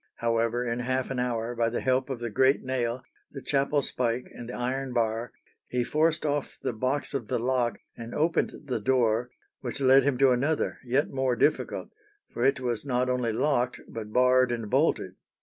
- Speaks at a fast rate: No, average, 190 wpm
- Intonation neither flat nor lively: No, narrow, 2.1 semitones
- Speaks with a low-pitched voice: Yes, low, 125 Hz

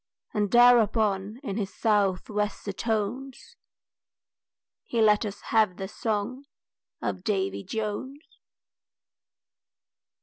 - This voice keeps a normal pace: No, slow, 95 wpm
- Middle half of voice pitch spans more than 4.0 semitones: No, average, 2.7 semitones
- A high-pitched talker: Yes, high, 210 Hz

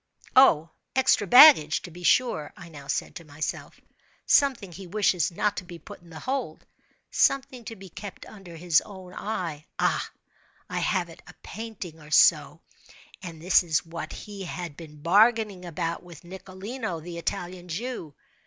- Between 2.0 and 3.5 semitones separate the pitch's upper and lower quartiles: No, average, 4.1 semitones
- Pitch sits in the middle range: Yes, medium, 180 Hz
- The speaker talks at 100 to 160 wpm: Yes, average, 150 wpm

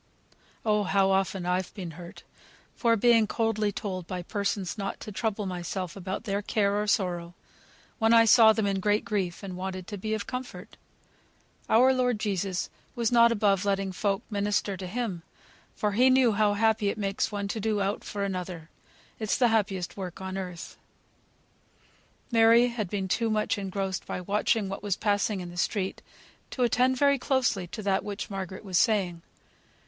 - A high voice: Yes, high, 200 Hz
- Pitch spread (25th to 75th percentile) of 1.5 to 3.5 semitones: Yes, average, 2.7 semitones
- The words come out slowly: No, average, 175 wpm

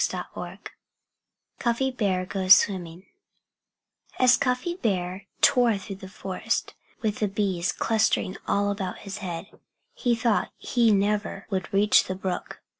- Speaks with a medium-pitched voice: No, high, 200 Hz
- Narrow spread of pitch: No, average, 3.4 semitones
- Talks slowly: Yes, slow, 130 wpm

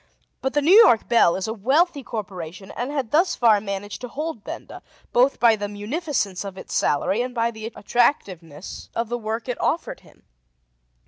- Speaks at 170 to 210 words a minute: Yes, average, 185 wpm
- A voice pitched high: Yes, high, 230 Hz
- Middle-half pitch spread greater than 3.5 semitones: Yes, average, 4.7 semitones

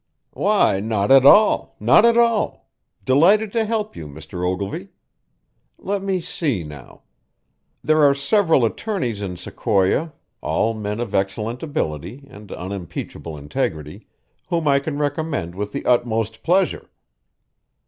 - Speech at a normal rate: No, slow, 130 wpm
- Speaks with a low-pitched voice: Yes, low, 120 Hz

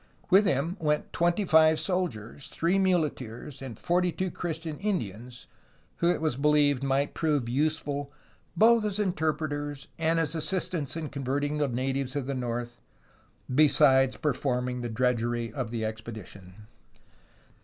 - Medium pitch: Yes, medium, 145 Hz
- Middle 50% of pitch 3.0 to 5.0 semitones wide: Yes, average, 4.6 semitones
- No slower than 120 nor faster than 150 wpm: Yes, average, 140 wpm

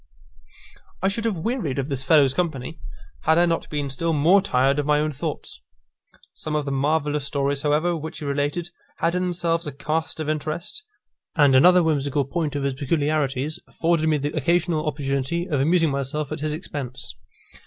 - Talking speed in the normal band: Yes, average, 180 wpm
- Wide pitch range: No, average, 3.0 semitones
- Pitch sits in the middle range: Yes, medium, 150 Hz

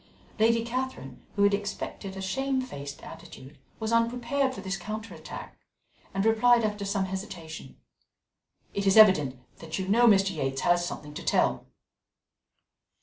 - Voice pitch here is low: No, high, 200 Hz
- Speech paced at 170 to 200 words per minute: No, average, 145 wpm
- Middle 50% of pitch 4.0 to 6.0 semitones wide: Yes, average, 4.9 semitones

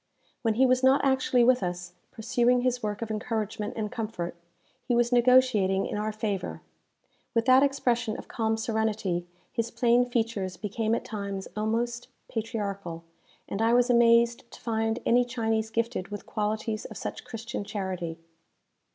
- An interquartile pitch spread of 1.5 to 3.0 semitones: Yes, narrow, 2.5 semitones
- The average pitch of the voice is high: Yes, high, 225 Hz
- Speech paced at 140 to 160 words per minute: Yes, average, 155 wpm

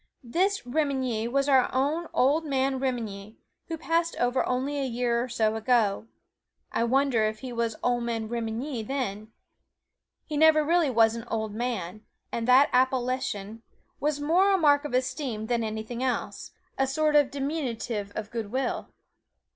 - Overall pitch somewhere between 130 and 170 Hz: No, very high, 250 Hz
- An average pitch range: Yes, average, 3.9 semitones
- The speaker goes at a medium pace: Yes, average, 160 wpm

